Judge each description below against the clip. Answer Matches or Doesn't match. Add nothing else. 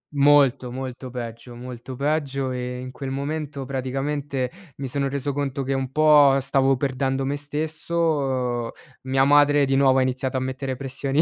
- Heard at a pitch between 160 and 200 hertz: Doesn't match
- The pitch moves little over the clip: Matches